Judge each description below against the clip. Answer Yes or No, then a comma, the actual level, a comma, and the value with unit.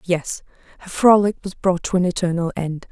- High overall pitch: No, medium, 180 Hz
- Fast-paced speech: No, average, 185 wpm